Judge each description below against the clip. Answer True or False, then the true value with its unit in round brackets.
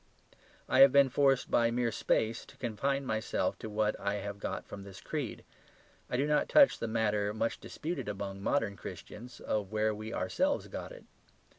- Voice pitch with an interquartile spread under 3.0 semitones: False (4.6 semitones)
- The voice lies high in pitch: False (110 Hz)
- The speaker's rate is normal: True (180 wpm)